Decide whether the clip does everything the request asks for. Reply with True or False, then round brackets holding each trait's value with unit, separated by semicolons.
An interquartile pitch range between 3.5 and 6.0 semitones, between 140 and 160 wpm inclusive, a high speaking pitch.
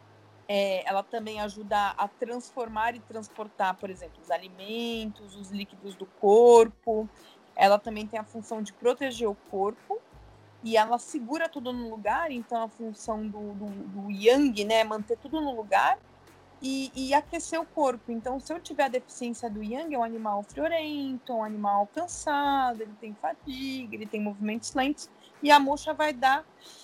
False (4.3 semitones; 170 wpm; 230 Hz)